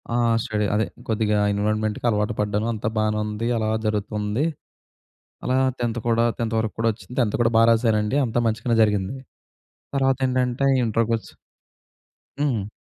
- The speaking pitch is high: No, low, 110 Hz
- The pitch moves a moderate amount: No, narrow, 1.8 semitones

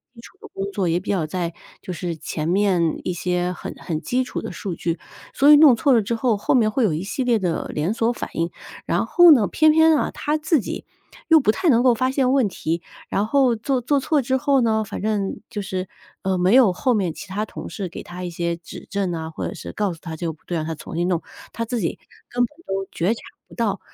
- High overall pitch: Yes, high, 205 Hz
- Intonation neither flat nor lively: No, wide, 6.2 semitones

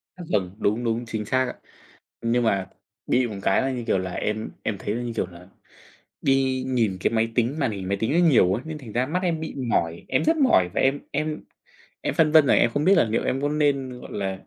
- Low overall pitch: Yes, low, 120 Hz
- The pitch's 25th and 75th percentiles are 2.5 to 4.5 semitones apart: No, average, 5.2 semitones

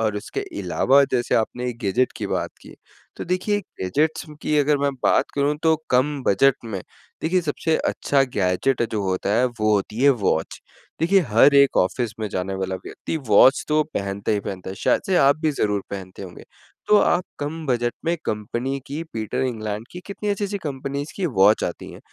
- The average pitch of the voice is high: No, low, 125 Hz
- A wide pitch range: Yes, wide, 6.5 semitones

